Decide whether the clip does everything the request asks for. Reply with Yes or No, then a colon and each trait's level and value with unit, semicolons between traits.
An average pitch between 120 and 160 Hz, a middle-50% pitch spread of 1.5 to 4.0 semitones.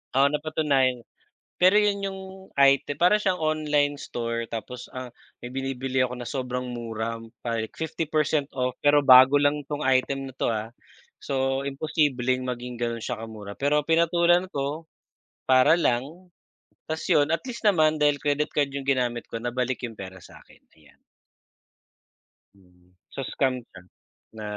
Yes: low, 135 Hz; average, 3.6 semitones